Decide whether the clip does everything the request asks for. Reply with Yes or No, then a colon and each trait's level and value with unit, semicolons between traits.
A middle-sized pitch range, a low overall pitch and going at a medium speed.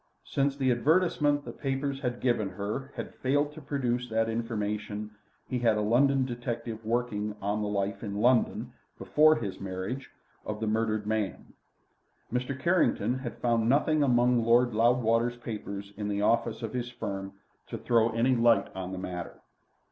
Yes: average, 3.3 semitones; low, 115 Hz; average, 165 wpm